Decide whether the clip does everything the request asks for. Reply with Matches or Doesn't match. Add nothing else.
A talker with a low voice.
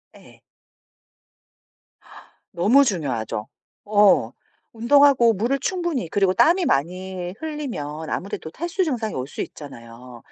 Doesn't match